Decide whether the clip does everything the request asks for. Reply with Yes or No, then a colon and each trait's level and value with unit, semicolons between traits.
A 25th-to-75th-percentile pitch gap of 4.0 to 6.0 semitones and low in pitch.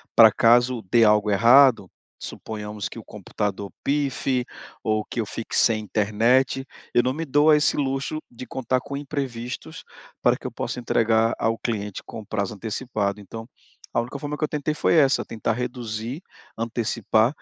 No: average, 3.6 semitones; low, 115 Hz